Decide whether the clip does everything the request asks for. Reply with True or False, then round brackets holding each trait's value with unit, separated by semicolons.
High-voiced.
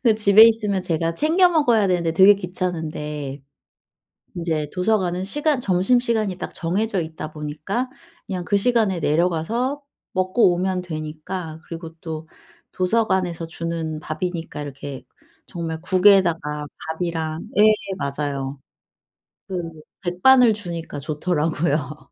False (175 Hz)